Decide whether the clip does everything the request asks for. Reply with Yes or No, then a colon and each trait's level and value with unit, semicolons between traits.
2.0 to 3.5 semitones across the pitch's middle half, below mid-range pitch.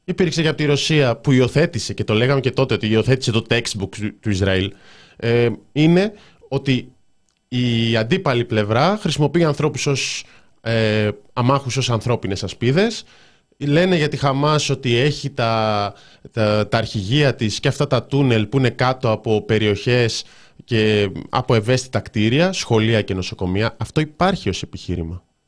No: average, 4.8 semitones; low, 120 Hz